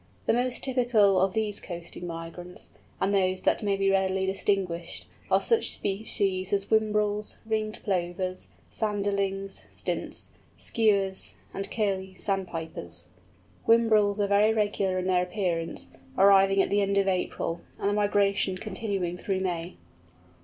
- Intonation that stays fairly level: Yes, narrow, 2.0 semitones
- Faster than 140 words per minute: No, slow, 135 wpm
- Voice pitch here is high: Yes, high, 195 Hz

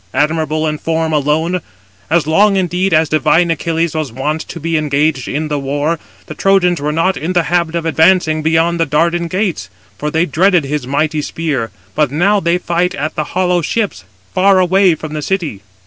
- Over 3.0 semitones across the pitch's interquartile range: No, average, 2.7 semitones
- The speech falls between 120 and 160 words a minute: No, average, 190 wpm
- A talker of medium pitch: Yes, medium, 160 Hz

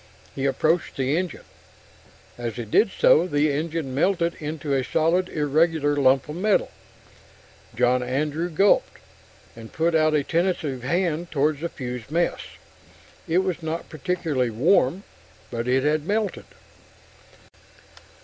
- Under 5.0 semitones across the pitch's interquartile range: Yes, average, 4.1 semitones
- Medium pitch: Yes, medium, 155 Hz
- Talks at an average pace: No, slow, 130 wpm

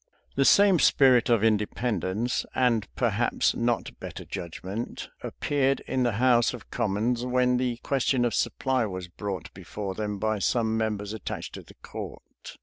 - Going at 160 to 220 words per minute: No, average, 150 wpm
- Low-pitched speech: Yes, low, 115 Hz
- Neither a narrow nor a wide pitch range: Yes, average, 3.4 semitones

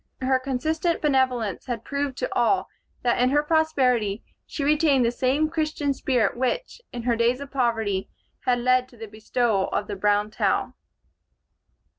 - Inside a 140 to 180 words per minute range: Yes, average, 160 wpm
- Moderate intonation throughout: Yes, average, 3.5 semitones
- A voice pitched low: No, very high, 255 Hz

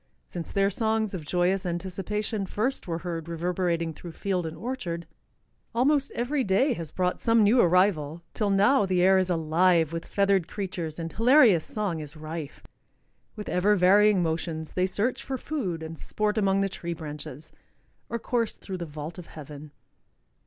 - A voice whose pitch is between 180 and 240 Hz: Yes, medium, 185 Hz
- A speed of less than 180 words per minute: Yes, average, 165 wpm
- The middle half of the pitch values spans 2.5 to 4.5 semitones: Yes, average, 4.1 semitones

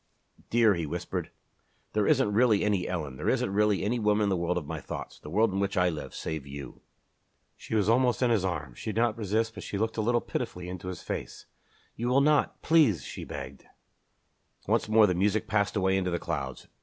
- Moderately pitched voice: No, low, 105 Hz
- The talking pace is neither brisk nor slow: No, fast, 220 wpm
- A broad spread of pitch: No, average, 3.7 semitones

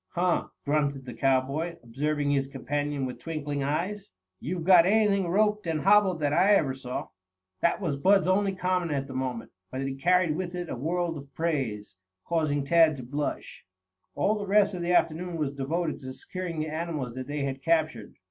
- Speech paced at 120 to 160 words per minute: No, average, 185 wpm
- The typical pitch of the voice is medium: Yes, medium, 155 Hz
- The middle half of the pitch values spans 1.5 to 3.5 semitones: No, average, 4.6 semitones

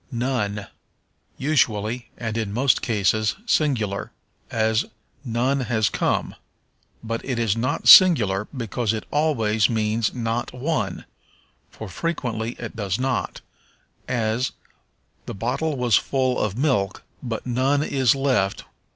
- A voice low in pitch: Yes, low, 115 Hz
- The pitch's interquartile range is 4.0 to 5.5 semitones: No, average, 3.3 semitones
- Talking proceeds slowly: Yes, slow, 120 wpm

